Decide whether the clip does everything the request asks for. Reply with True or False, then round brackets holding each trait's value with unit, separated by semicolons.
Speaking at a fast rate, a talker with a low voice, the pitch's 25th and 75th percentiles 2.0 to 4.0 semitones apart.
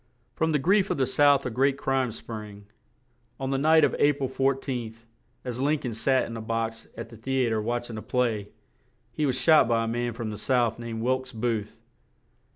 True (215 wpm; 125 Hz; 2.9 semitones)